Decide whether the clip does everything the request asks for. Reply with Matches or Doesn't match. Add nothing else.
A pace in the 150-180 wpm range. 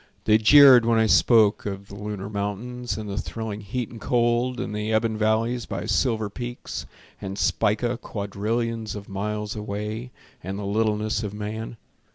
Matches